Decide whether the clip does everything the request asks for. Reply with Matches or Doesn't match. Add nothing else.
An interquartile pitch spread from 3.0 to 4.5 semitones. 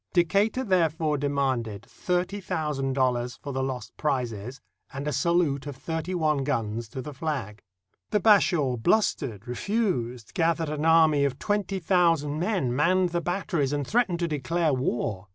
Doesn't match